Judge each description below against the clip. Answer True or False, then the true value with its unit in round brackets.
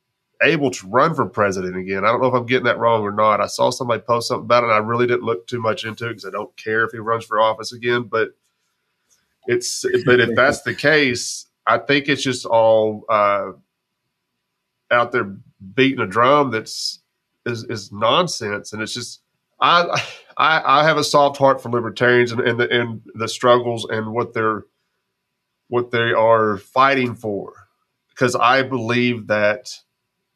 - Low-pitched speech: True (120 Hz)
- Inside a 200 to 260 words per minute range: False (185 wpm)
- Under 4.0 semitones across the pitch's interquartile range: True (2.4 semitones)